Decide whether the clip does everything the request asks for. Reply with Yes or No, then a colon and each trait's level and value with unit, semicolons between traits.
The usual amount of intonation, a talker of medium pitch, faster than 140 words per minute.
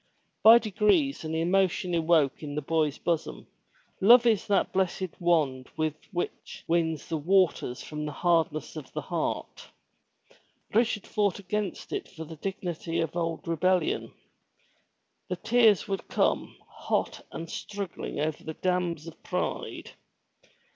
No: average, 3.7 semitones; medium, 175 Hz; slow, 135 wpm